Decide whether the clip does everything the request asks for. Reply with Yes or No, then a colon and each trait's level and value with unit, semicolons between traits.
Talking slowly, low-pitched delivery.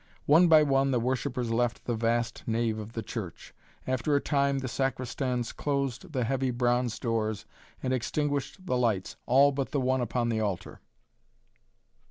No: average, 165 wpm; low, 125 Hz